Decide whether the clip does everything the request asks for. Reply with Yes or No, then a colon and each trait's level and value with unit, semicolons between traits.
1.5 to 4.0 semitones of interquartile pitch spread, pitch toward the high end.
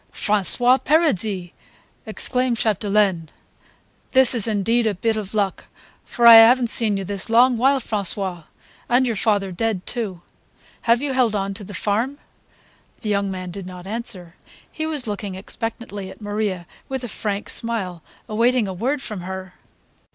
Yes: average, 3.7 semitones; high, 215 Hz